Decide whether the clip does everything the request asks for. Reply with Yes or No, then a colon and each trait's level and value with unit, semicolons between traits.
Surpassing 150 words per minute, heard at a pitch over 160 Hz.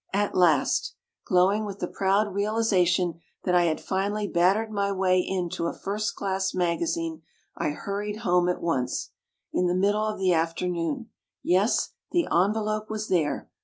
Yes: average, 165 wpm; high, 190 Hz